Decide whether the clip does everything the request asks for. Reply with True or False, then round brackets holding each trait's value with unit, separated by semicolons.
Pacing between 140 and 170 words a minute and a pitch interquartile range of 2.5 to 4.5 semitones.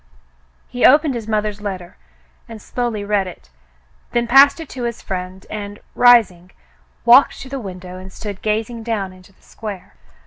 True (165 wpm; 4.0 semitones)